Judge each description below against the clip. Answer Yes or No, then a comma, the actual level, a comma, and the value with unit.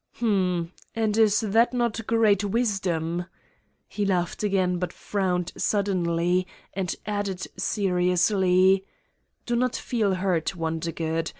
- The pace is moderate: No, slow, 110 wpm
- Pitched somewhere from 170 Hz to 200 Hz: Yes, high, 190 Hz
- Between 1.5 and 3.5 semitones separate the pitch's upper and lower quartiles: Yes, average, 2.9 semitones